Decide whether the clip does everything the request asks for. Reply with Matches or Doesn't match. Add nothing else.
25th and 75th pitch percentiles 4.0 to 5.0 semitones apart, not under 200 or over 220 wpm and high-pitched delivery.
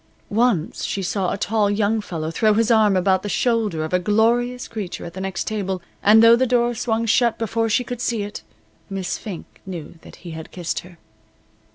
Doesn't match